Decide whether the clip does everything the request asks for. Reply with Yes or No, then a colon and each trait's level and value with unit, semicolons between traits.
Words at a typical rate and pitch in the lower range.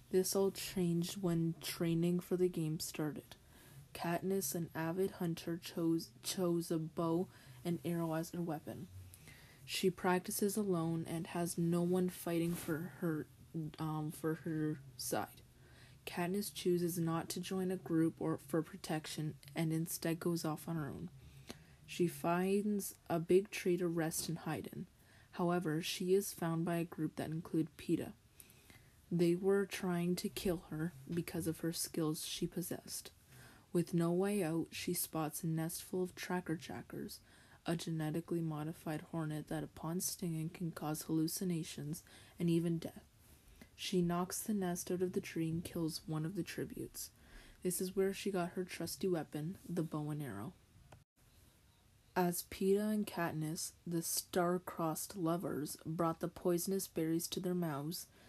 No: average, 155 wpm; medium, 170 Hz